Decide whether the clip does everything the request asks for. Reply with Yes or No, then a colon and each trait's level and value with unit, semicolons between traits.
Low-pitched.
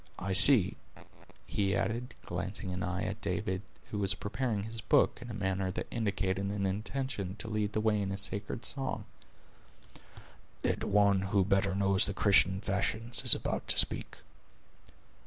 Yes: low, 100 Hz